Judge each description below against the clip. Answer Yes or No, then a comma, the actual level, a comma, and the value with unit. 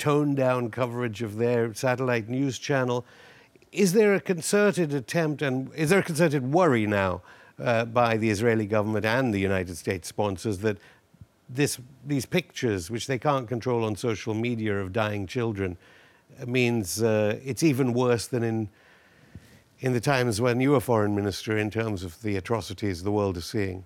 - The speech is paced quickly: No, average, 170 wpm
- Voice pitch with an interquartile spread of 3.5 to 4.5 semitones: Yes, average, 3.8 semitones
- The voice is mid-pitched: No, low, 120 Hz